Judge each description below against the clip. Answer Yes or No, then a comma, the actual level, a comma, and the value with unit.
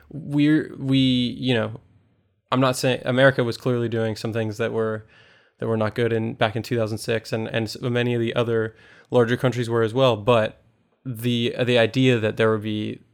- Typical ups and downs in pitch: No, narrow, 2.1 semitones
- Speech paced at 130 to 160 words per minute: No, average, 195 wpm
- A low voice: Yes, low, 115 Hz